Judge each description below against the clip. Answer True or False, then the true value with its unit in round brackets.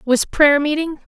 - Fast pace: False (155 wpm)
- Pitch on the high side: True (295 Hz)